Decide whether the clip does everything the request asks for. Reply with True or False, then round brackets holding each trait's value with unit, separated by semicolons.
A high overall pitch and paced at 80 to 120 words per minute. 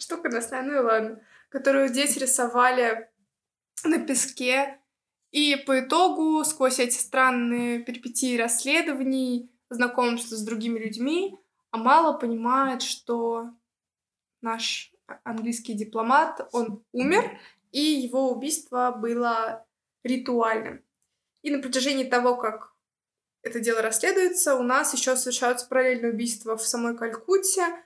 True (250 Hz; 110 wpm)